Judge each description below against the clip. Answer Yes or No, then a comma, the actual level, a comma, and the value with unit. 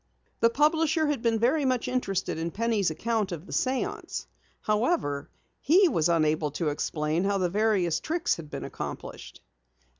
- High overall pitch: Yes, high, 210 Hz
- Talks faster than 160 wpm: No, average, 155 wpm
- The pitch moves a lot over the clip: Yes, wide, 7.7 semitones